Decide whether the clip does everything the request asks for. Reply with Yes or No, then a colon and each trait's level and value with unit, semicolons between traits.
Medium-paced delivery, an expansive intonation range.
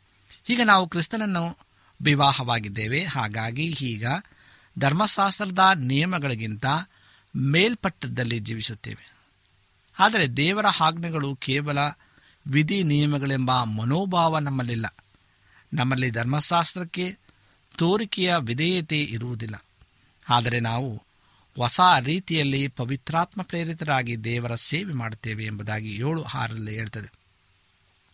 Yes: average, 75 wpm; wide, 6.8 semitones